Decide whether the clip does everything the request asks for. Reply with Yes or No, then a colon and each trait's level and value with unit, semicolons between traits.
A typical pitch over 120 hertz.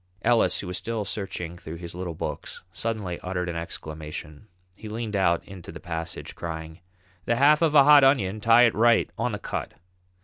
No: very low, 95 Hz